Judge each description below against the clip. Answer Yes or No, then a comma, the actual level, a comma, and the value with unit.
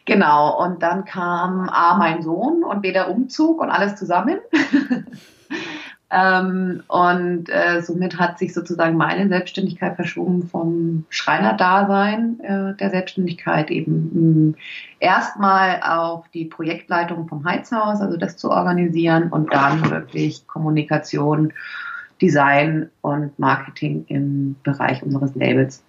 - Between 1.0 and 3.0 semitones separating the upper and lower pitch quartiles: No, average, 3.4 semitones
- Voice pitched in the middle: Yes, medium, 175 Hz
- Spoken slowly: Yes, slow, 115 wpm